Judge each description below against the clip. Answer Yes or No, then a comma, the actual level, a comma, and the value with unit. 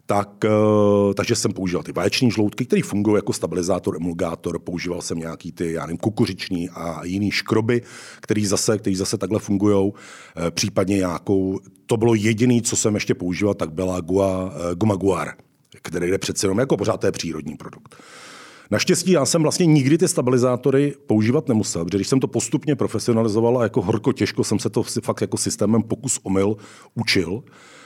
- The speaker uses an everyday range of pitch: Yes, average, 3.7 semitones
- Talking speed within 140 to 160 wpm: No, fast, 170 wpm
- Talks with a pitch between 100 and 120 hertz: Yes, low, 105 Hz